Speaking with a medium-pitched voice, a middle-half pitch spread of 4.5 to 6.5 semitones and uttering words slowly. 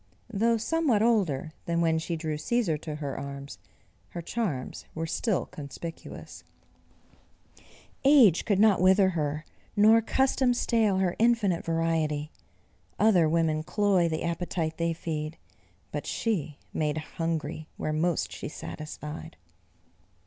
Yes: medium, 165 Hz; average, 5.1 semitones; slow, 125 wpm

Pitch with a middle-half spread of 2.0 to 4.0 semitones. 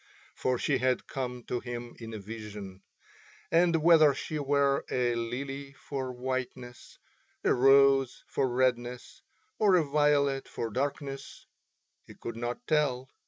Yes: narrow, 2.6 semitones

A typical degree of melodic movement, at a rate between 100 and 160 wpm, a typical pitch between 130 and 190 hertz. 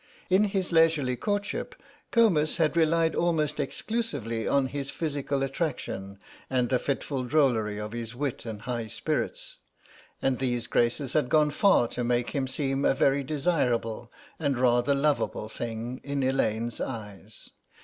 Yes: average, 4.2 semitones; average, 145 wpm; low, 135 Hz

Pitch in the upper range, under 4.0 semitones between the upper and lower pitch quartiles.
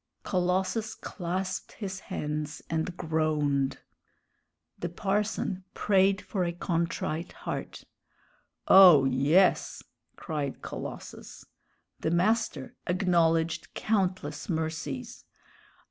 No: medium, 170 Hz; average, 3.4 semitones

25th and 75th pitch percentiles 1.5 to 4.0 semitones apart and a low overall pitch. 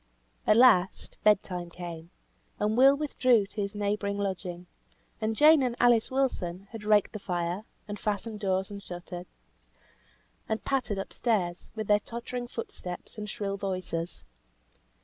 No: average, 3.7 semitones; high, 205 Hz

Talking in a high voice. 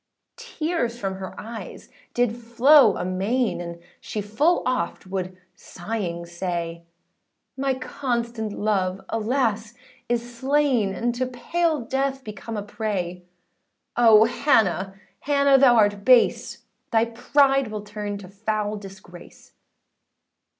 Yes: high, 225 Hz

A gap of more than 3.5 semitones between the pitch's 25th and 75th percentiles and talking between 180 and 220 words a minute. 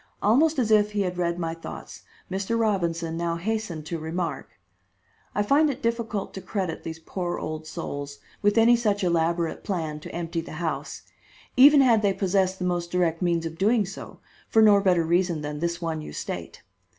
Yes: average, 4.1 semitones; average, 185 wpm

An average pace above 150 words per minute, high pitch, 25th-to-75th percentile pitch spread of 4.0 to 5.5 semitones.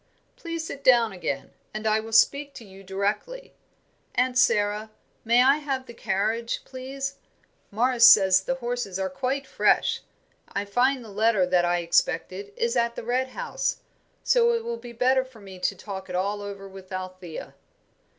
Yes: average, 170 wpm; high, 230 Hz; average, 5.0 semitones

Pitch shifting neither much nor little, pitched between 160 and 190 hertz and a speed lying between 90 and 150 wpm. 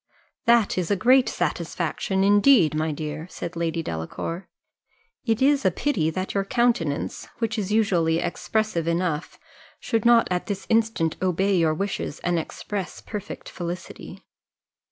Yes: average, 4.9 semitones; medium, 185 Hz; average, 140 wpm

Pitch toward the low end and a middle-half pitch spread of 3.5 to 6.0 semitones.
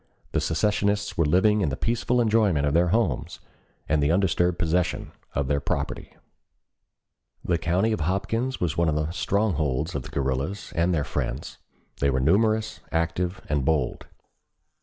Yes: very low, 85 Hz; wide, 5.5 semitones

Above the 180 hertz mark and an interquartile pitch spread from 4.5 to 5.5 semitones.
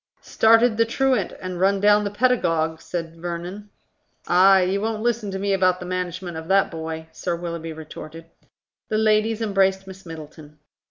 No: high, 190 Hz; average, 3.9 semitones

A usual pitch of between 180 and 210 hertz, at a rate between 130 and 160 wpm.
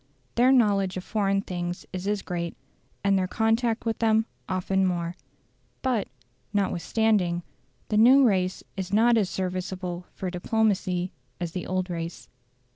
Yes: high, 190 Hz; average, 140 wpm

